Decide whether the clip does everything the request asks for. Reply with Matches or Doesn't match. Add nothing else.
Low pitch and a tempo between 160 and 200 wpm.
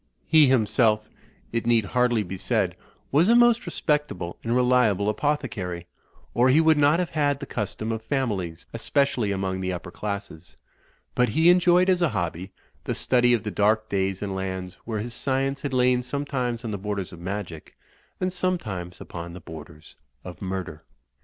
Matches